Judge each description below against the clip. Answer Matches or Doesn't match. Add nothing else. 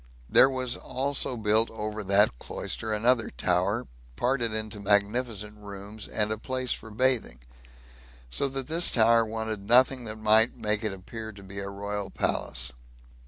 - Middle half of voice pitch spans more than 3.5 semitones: Doesn't match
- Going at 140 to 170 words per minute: Matches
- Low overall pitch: Matches